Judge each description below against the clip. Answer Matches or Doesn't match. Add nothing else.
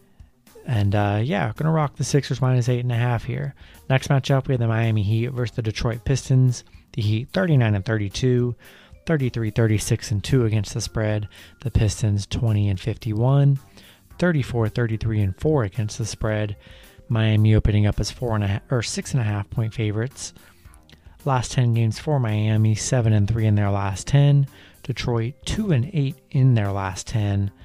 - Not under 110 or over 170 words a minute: Doesn't match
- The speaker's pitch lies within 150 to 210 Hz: Doesn't match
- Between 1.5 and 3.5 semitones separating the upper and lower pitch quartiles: Doesn't match